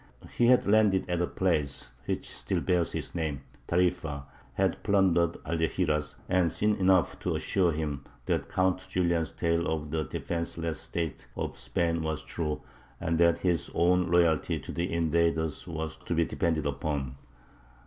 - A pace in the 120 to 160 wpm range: Yes, average, 155 wpm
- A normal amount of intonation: No, narrow, 2.3 semitones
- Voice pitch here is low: Yes, very low, 85 Hz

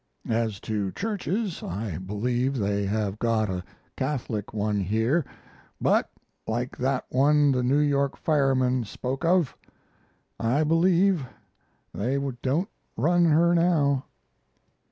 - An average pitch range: No, wide, 5.9 semitones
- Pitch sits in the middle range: No, low, 130 Hz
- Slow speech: Yes, slow, 115 wpm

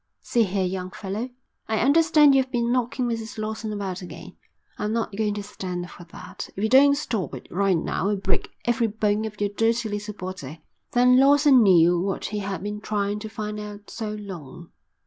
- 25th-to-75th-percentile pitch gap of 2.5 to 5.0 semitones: Yes, average, 3.1 semitones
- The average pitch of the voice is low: No, high, 210 Hz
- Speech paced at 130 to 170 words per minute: No, average, 195 wpm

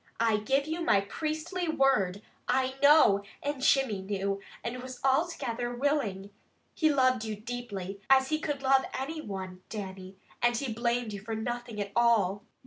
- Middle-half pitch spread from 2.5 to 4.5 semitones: No, average, 5.0 semitones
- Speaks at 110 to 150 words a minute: No, average, 160 wpm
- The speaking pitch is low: No, high, 240 Hz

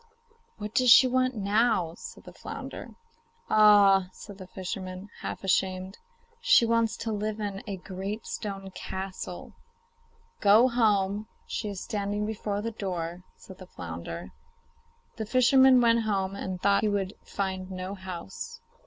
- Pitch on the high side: Yes, high, 200 Hz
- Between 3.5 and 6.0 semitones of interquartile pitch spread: No, narrow, 2.6 semitones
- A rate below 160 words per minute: Yes, average, 145 wpm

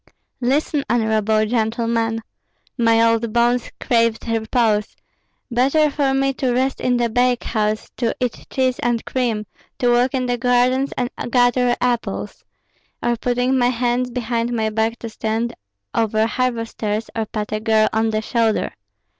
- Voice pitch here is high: Yes, high, 235 Hz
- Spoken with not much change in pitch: Yes, narrow, 1.9 semitones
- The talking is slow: No, average, 145 wpm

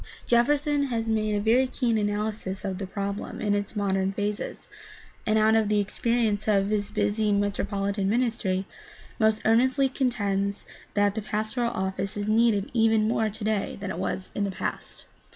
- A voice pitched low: No, high, 210 Hz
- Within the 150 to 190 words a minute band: Yes, average, 165 wpm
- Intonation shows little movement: Yes, narrow, 2.0 semitones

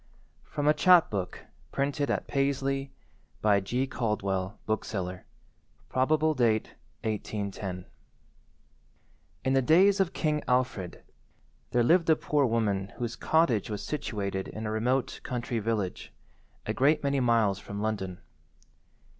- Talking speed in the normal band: No, slow, 120 wpm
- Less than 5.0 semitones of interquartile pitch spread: No, average, 5.3 semitones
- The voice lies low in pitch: Yes, low, 120 Hz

